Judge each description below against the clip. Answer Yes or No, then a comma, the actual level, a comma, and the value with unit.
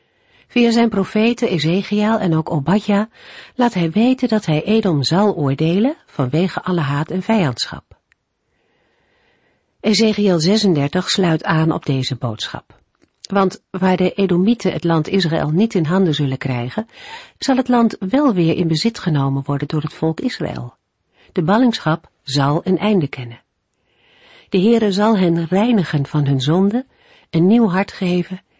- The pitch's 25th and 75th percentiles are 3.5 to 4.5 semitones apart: No, wide, 5.4 semitones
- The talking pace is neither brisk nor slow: Yes, average, 145 wpm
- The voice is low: No, medium, 185 Hz